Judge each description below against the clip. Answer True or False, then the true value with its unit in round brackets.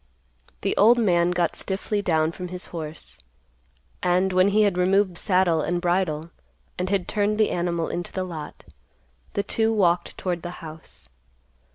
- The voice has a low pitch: False (180 Hz)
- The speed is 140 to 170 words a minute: True (160 wpm)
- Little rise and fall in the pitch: True (2.3 semitones)